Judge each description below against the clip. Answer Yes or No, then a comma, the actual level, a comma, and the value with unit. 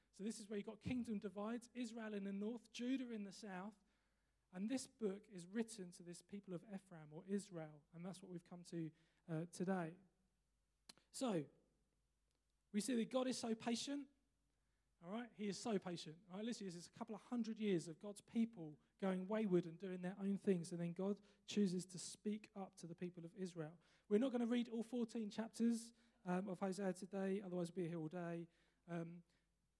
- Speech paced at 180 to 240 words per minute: Yes, fast, 205 wpm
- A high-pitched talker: Yes, high, 195 Hz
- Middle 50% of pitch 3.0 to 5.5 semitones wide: Yes, average, 3.9 semitones